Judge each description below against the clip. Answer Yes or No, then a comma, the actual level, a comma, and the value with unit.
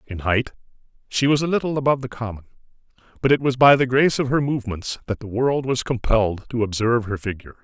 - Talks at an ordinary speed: No, fast, 210 wpm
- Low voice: Yes, low, 120 Hz